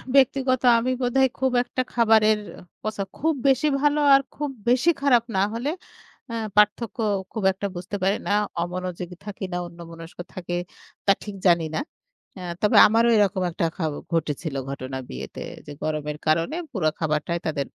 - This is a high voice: Yes, high, 200 Hz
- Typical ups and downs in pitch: No, wide, 6.5 semitones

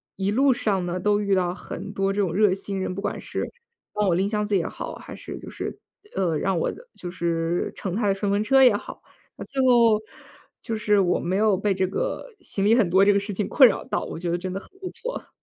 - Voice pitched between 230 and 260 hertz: No, high, 200 Hz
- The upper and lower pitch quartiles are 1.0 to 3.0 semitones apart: Yes, narrow, 2.4 semitones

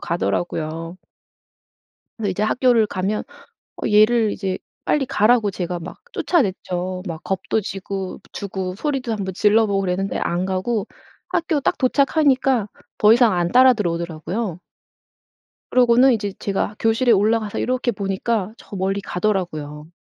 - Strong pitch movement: No, average, 4.2 semitones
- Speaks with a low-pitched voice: No, high, 205 Hz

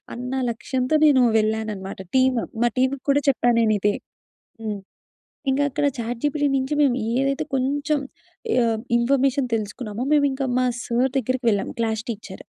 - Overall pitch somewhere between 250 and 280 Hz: Yes, very high, 255 Hz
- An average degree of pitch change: Yes, average, 3.6 semitones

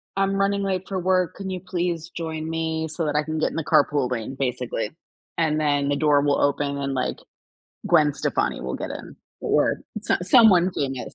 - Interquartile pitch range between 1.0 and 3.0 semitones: No, average, 4.2 semitones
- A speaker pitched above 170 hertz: No, medium, 160 Hz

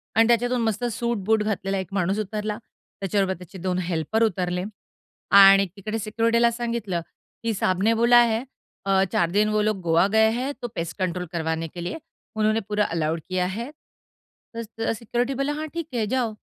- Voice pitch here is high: Yes, high, 210 Hz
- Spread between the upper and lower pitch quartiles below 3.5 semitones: No, average, 3.8 semitones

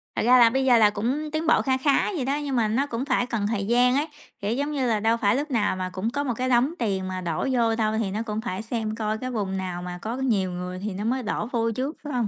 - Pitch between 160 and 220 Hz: No, high, 230 Hz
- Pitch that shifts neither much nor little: Yes, average, 3.9 semitones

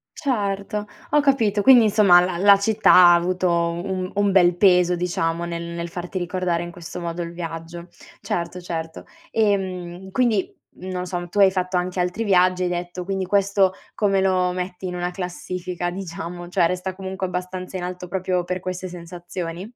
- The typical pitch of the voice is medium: Yes, medium, 180 Hz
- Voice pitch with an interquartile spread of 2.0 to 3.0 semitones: No, narrow, 1.6 semitones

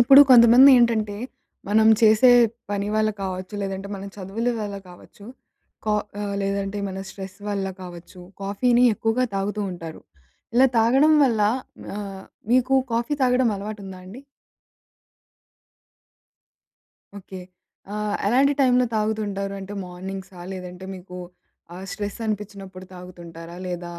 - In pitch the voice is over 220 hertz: No, high, 200 Hz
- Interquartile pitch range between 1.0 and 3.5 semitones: Yes, average, 3.2 semitones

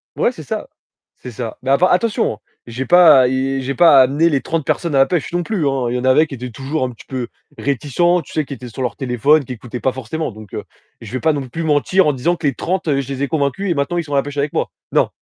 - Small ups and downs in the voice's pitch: No, average, 3.7 semitones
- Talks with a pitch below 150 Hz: Yes, medium, 140 Hz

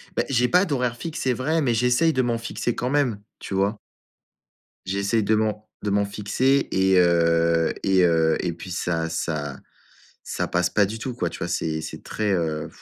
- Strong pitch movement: Yes, wide, 6.1 semitones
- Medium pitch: No, low, 100 Hz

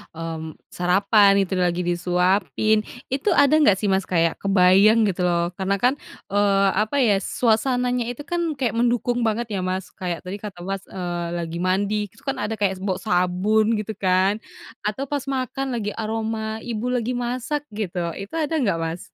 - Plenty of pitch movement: No, average, 4.3 semitones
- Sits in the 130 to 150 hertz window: No, high, 205 Hz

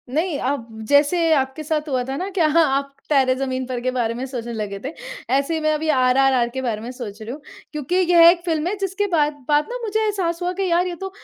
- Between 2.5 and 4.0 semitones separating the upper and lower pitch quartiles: No, average, 4.7 semitones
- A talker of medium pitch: No, very high, 290 Hz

